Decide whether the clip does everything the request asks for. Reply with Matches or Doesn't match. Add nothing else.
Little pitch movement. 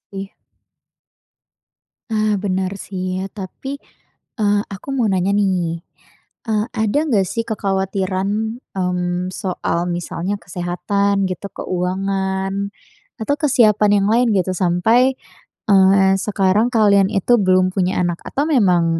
Matches